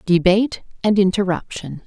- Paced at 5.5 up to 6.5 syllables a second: No, 5.0 syllables/s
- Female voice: Yes, female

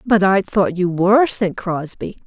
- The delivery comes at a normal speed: Yes, average, 185 wpm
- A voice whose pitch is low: No, high, 195 Hz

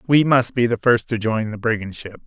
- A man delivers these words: Yes, male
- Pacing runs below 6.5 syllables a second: Yes, 5.3 syllables/s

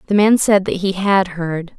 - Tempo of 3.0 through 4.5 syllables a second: Yes, 4.4 syllables/s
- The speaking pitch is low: No, high, 190 Hz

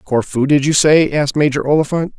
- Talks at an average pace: Yes, average, 190 wpm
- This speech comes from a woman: No, male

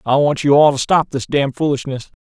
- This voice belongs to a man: Yes, male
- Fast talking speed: Yes, fast, 245 wpm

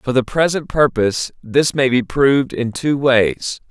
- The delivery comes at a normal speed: Yes, average, 180 wpm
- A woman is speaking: No, male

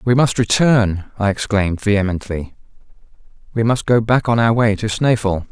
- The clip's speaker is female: No, male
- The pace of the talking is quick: No, average, 165 wpm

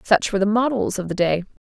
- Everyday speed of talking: No, fast, 260 wpm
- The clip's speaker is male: No, female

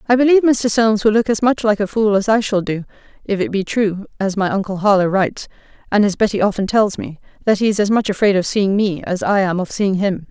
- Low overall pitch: No, high, 205 Hz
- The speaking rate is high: Yes, fast, 260 wpm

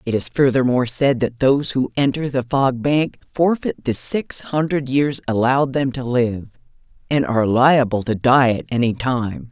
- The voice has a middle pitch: No, low, 130 Hz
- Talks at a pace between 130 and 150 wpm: No, average, 175 wpm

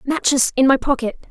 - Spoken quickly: No, average, 185 wpm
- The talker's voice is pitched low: No, very high, 265 Hz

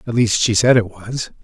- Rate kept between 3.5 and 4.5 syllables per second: No, 5.0 syllables/s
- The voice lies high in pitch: No, low, 110 Hz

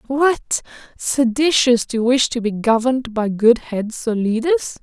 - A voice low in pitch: No, high, 245 Hz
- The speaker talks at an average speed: Yes, average, 150 wpm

